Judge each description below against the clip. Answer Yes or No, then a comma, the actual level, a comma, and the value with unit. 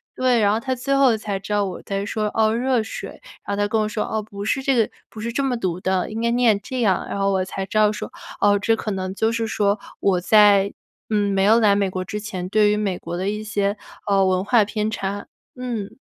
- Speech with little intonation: Yes, narrow, 2.2 semitones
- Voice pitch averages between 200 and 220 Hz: Yes, high, 210 Hz